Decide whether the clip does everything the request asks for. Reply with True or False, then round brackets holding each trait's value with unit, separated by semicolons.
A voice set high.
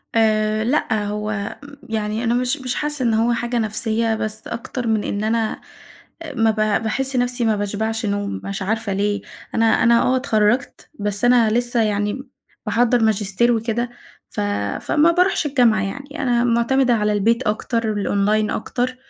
True (225 Hz)